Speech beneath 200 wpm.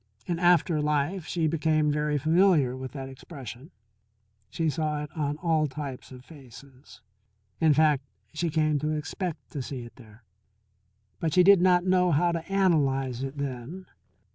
Yes: average, 160 wpm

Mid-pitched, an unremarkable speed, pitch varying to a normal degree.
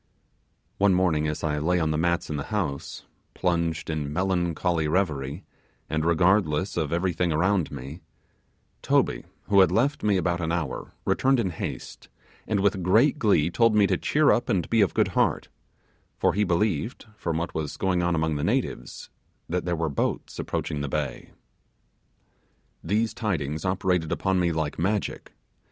No: very low, 85 Hz; average, 165 wpm; average, 3.9 semitones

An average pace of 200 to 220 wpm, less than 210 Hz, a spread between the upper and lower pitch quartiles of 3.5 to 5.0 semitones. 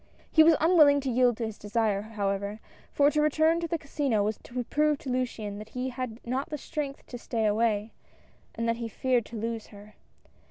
No: fast, 205 wpm; high, 240 Hz; average, 4.6 semitones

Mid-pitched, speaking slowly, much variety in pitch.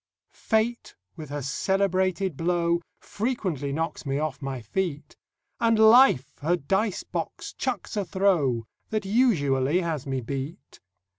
Yes: medium, 170 Hz; slow, 130 wpm; wide, 6.1 semitones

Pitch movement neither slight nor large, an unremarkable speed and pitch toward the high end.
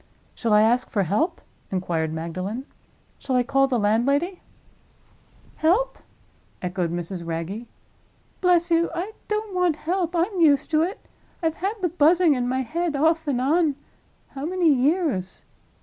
No: wide, 7.9 semitones; average, 145 wpm; very high, 285 Hz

